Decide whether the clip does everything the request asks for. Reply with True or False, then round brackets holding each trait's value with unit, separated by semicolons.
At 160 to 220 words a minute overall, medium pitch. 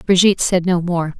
True (200 wpm; 175 Hz)